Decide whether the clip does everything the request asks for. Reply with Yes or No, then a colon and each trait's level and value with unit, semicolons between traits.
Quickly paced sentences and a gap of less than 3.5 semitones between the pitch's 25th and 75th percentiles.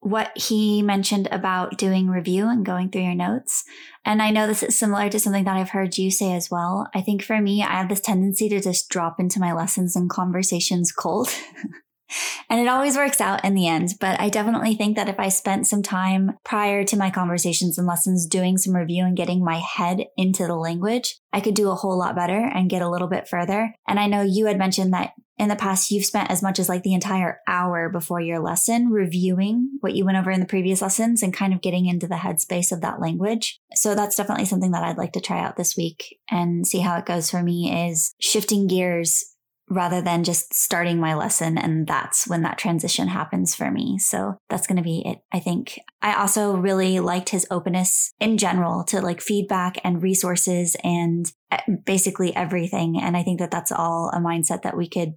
Yes: fast, 220 wpm; average, 2.8 semitones